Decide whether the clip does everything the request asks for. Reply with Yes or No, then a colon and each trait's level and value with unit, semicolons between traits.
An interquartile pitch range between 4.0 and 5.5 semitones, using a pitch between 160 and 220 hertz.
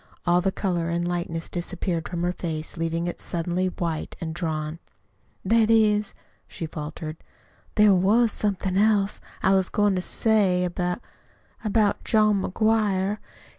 No: average, 3.4 semitones; medium, 185 Hz